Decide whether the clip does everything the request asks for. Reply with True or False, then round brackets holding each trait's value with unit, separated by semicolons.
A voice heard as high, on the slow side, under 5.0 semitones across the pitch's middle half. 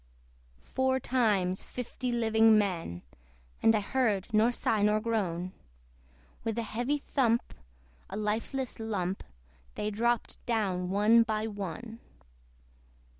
True (220 Hz; 110 wpm; 2.7 semitones)